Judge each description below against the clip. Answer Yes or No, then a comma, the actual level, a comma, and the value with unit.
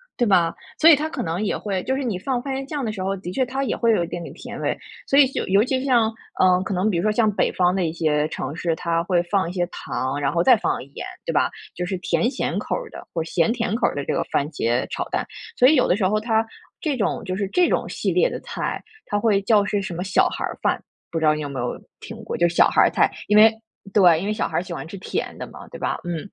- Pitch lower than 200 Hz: Yes, high, 190 Hz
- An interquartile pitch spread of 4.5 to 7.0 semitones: Yes, average, 5.0 semitones